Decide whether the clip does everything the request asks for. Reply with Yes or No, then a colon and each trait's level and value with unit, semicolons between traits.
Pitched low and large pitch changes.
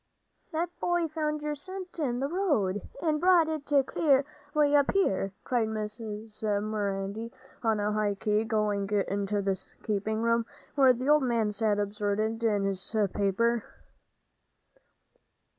No: high, 220 Hz; wide, 5.9 semitones